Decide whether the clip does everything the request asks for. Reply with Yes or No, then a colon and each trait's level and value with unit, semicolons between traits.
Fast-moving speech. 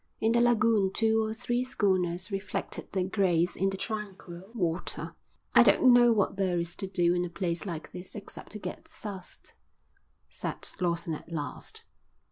No: average, 170 wpm